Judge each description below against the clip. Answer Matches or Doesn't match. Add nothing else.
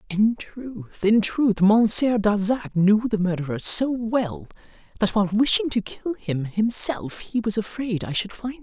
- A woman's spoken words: Matches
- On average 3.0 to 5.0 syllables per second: Matches